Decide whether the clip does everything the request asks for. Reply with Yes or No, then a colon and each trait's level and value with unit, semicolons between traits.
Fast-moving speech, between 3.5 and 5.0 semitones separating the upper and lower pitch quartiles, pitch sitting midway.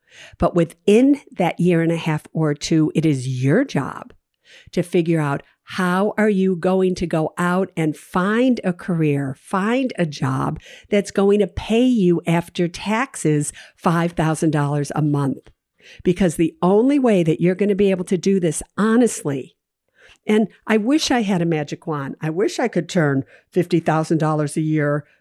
No: average, 165 wpm; average, 4.5 semitones; medium, 175 Hz